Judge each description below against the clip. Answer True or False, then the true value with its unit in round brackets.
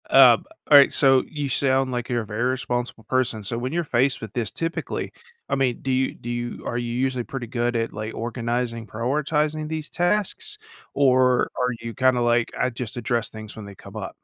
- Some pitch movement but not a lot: False (2.2 semitones)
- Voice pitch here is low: True (125 Hz)